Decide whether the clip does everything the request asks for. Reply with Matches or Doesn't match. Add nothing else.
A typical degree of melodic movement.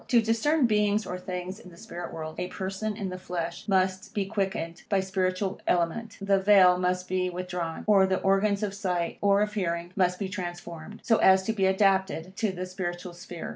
Doesn't match